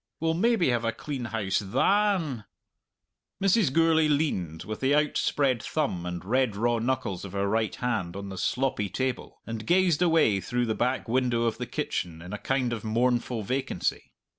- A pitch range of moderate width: No, wide, 5.7 semitones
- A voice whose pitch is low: Yes, low, 120 Hz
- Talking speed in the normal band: Yes, average, 175 wpm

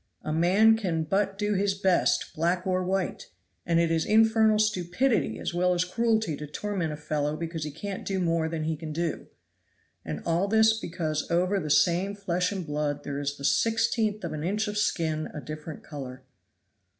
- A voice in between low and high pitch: Yes, medium, 175 Hz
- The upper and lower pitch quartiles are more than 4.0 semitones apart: Yes, average, 4.7 semitones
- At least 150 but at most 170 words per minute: No, average, 190 wpm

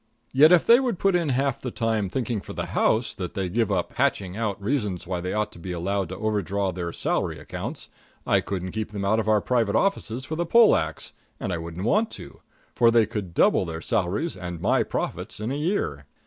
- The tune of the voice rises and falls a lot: Yes, wide, 5.7 semitones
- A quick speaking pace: Yes, fast, 230 wpm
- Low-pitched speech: Yes, low, 105 Hz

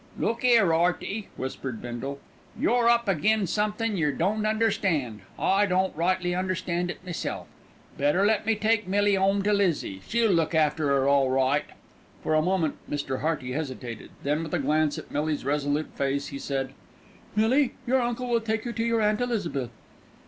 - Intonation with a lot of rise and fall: Yes, wide, 6.8 semitones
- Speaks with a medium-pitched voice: Yes, medium, 180 Hz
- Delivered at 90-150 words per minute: No, average, 170 wpm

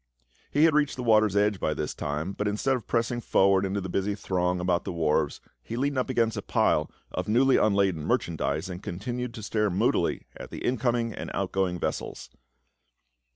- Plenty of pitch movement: No, average, 4.7 semitones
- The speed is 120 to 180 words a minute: No, average, 190 wpm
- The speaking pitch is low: Yes, low, 100 Hz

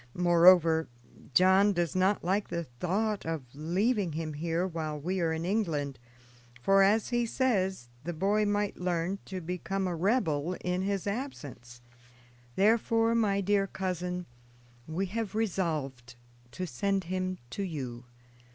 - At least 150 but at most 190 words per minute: No, average, 140 wpm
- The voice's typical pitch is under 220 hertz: Yes, medium, 185 Hz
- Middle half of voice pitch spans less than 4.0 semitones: Yes, average, 3.6 semitones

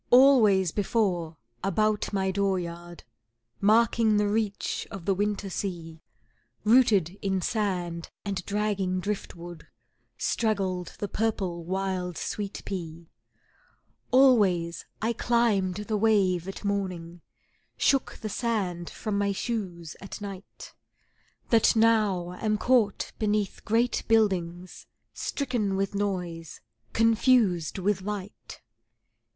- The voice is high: Yes, high, 200 Hz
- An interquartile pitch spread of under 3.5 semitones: Yes, average, 3.1 semitones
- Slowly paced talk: Yes, slow, 110 wpm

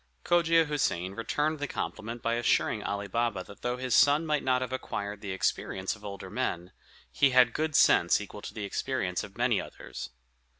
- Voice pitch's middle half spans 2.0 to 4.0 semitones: No, average, 5.1 semitones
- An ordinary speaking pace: Yes, average, 185 wpm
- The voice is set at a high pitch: No, low, 115 Hz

